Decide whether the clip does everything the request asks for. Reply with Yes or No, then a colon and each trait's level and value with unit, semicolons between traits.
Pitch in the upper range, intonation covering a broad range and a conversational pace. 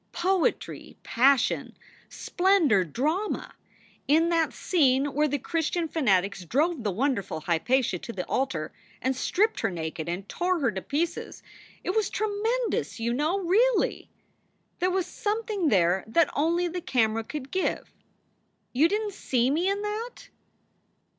Yes: very high, 305 Hz; wide, 7.9 semitones; average, 145 wpm